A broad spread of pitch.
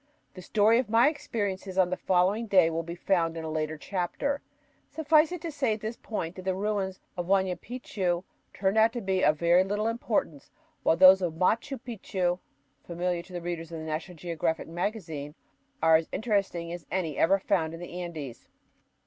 No: average, 4.1 semitones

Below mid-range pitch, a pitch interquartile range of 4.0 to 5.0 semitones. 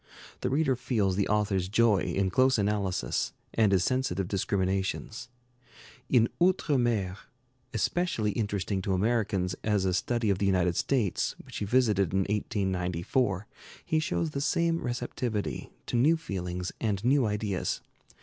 Yes: low, 105 Hz; average, 4.3 semitones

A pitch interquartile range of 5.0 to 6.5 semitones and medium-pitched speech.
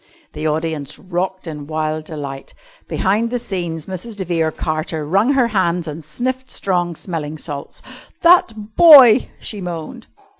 Yes: wide, 5.4 semitones; medium, 175 Hz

